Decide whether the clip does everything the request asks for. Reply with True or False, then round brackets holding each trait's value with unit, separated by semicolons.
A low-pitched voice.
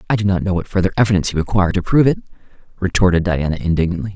True (95 Hz)